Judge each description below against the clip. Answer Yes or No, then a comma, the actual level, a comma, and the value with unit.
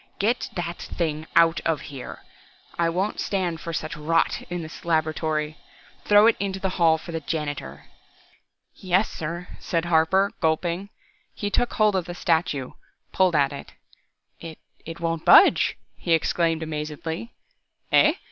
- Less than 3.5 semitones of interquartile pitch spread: Yes, narrow, 2.4 semitones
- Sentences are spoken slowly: No, average, 145 wpm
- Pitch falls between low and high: Yes, medium, 165 Hz